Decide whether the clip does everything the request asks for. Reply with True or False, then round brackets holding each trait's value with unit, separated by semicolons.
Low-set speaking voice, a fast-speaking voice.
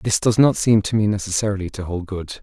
True (100 Hz; 250 wpm)